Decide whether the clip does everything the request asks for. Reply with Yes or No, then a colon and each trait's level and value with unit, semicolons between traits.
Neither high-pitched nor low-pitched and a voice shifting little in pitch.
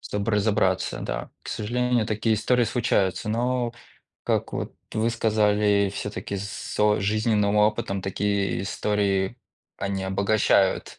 No: low, 105 Hz; narrow, 2.0 semitones